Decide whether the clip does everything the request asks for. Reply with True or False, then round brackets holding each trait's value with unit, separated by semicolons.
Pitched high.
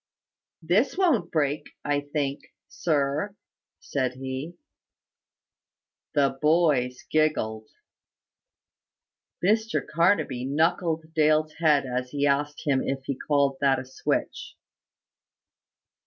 False (145 Hz)